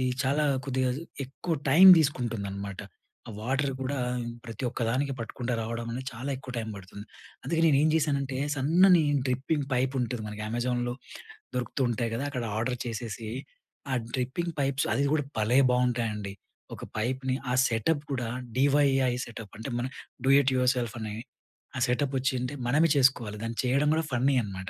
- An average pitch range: Yes, average, 3.0 semitones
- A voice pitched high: No, low, 125 Hz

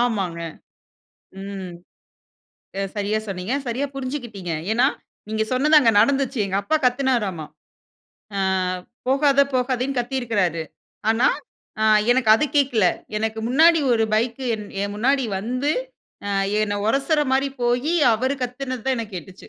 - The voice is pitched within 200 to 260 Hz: Yes, high, 240 Hz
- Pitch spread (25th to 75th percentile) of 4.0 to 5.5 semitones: Yes, average, 4.3 semitones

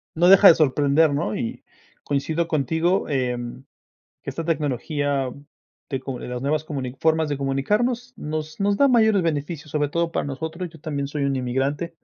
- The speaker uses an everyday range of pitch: Yes, average, 3.4 semitones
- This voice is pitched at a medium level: Yes, medium, 150 Hz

